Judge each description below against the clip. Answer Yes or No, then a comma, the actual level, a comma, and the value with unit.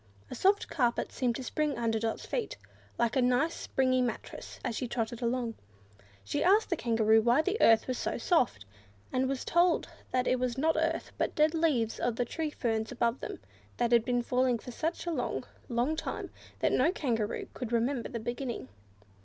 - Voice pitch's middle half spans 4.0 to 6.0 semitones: Yes, average, 4.4 semitones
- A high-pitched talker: Yes, very high, 250 Hz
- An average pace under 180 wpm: No, average, 195 wpm